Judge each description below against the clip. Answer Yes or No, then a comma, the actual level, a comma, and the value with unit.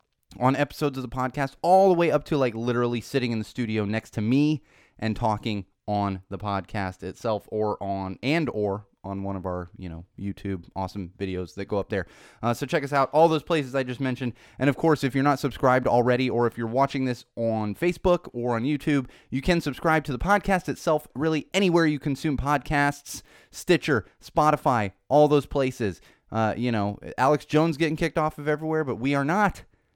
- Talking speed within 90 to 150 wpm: No, fast, 205 wpm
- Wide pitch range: Yes, wide, 6.3 semitones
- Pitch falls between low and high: No, low, 125 Hz